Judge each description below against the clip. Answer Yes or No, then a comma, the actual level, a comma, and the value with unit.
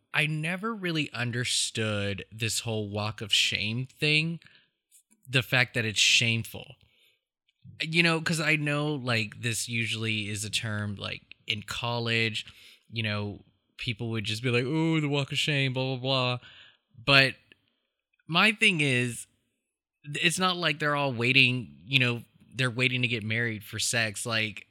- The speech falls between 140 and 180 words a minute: Yes, average, 155 wpm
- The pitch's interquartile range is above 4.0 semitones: Yes, average, 4.7 semitones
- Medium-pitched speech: No, low, 120 Hz